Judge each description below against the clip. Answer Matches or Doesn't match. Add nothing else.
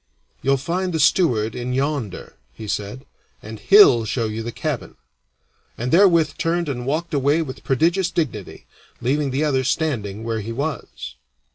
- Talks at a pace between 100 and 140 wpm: Doesn't match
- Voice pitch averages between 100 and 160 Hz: Matches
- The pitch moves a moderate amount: Doesn't match